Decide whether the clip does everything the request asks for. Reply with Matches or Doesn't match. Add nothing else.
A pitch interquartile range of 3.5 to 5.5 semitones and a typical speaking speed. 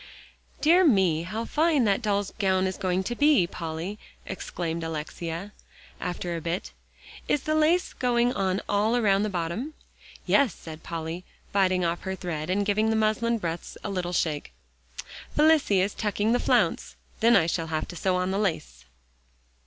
Matches